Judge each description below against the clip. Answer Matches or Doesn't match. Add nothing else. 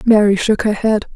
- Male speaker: Doesn't match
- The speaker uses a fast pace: Matches